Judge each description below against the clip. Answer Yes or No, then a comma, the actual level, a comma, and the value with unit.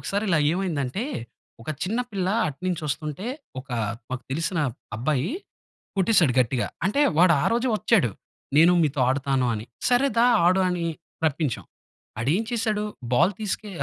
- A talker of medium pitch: Yes, medium, 170 Hz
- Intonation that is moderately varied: No, wide, 6.8 semitones